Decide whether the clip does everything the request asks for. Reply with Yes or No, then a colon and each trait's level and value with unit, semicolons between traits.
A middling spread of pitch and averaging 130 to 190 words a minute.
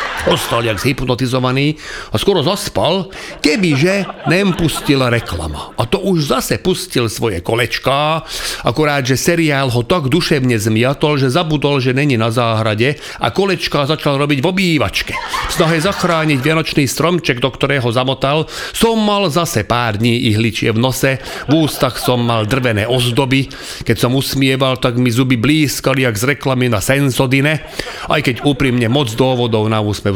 Yes: average, 4.3 semitones; average, 155 wpm